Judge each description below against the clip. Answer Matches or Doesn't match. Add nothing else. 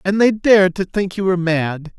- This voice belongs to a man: Matches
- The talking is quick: Matches